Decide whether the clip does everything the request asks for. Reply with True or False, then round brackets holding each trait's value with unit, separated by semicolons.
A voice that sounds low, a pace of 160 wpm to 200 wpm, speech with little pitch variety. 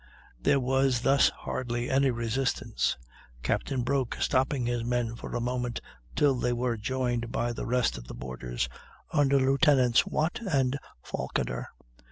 False (125 Hz; 145 wpm; 2.2 semitones)